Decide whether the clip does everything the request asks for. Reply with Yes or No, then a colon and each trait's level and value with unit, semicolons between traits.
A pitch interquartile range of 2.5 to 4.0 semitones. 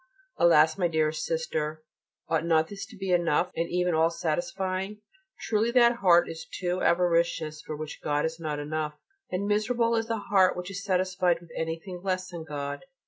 Yes: average, 3.1 semitones